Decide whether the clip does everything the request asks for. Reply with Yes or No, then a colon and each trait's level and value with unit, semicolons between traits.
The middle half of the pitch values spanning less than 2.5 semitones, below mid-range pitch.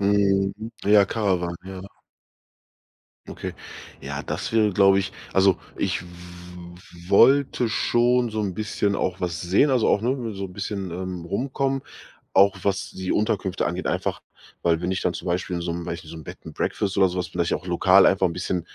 No: average, 2.8 semitones; very low, 95 Hz